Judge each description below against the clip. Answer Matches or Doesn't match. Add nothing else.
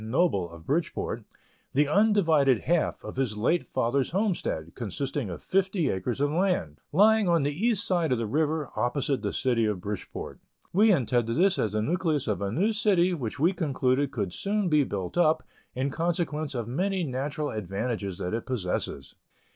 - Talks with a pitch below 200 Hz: Matches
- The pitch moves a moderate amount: Doesn't match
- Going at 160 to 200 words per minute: Matches